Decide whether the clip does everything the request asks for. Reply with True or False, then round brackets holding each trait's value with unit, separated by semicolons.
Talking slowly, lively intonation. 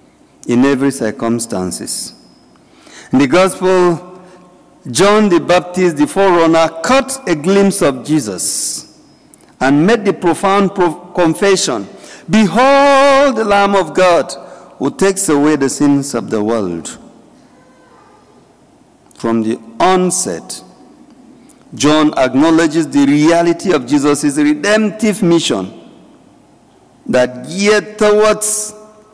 True (100 wpm; 6.0 semitones)